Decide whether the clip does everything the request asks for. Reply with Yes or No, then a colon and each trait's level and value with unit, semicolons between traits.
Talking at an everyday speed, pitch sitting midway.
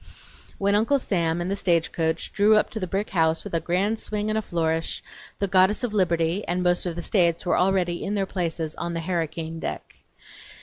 No: fast, 210 wpm; medium, 180 Hz